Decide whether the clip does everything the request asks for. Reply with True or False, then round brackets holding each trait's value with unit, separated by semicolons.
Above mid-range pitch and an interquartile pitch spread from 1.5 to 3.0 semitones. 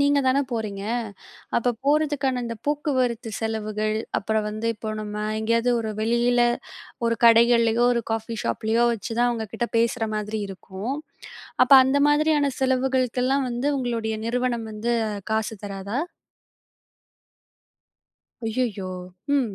True (235 Hz; 2.6 semitones)